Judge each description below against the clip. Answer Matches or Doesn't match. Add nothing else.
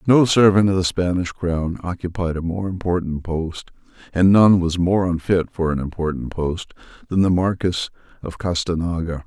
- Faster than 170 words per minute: Doesn't match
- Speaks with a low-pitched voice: Matches